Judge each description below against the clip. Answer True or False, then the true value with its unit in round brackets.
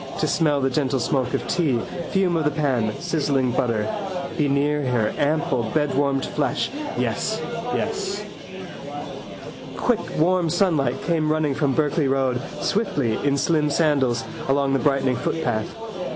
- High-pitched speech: False (140 Hz)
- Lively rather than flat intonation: False (3.0 semitones)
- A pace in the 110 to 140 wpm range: True (135 wpm)